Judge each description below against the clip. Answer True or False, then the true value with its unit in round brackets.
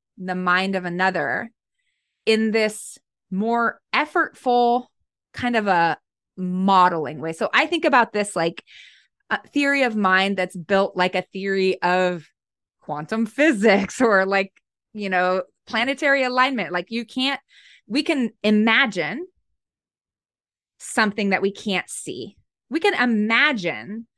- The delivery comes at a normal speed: False (125 wpm)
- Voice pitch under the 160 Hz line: False (215 Hz)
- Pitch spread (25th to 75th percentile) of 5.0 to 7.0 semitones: True (5.3 semitones)